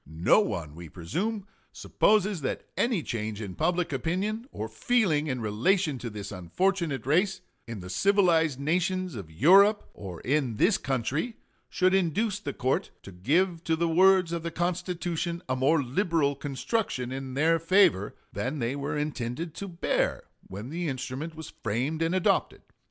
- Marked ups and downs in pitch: Yes, wide, 6.5 semitones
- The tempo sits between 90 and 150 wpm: No, average, 160 wpm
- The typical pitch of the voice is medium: Yes, medium, 160 Hz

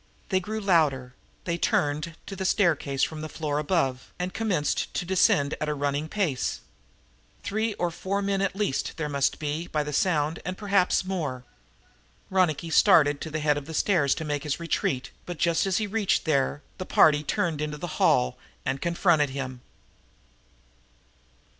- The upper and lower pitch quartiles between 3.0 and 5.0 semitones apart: Yes, average, 4.2 semitones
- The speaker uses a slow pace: No, average, 170 wpm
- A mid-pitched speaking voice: Yes, medium, 160 Hz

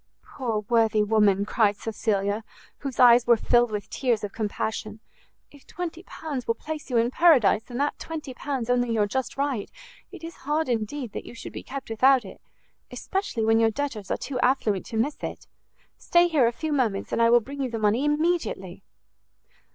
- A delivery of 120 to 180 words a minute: No, average, 190 wpm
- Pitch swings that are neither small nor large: Yes, average, 4.4 semitones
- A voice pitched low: No, high, 240 Hz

